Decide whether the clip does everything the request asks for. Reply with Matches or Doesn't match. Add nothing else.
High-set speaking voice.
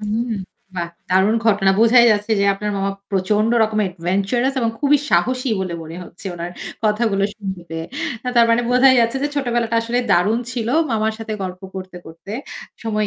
Matches